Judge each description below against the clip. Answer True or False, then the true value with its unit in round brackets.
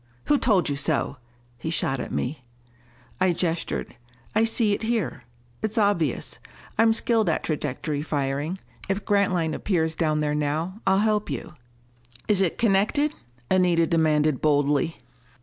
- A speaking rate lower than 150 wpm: True (140 wpm)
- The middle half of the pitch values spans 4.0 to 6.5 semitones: True (5.4 semitones)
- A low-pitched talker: False (170 Hz)